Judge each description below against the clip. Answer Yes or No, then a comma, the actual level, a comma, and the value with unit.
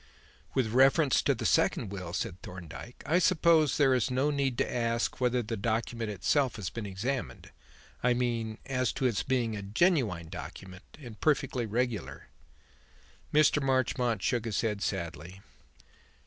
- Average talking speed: Yes, average, 150 wpm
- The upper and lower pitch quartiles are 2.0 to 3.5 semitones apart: No, average, 4.1 semitones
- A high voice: No, low, 120 Hz